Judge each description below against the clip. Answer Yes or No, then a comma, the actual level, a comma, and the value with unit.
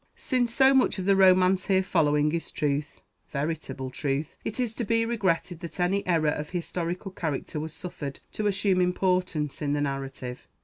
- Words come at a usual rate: Yes, average, 175 wpm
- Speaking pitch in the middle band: Yes, medium, 175 Hz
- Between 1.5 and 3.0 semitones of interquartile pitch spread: No, average, 4.5 semitones